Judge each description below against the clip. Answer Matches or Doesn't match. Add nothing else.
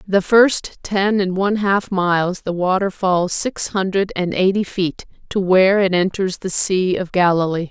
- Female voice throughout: Matches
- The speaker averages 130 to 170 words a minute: Doesn't match